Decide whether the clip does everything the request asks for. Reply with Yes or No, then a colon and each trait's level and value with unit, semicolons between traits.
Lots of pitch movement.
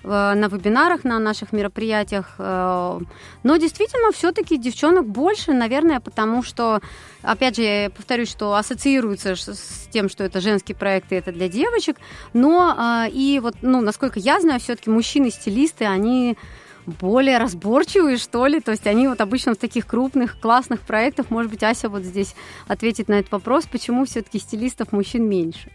No: average, 4.3 semitones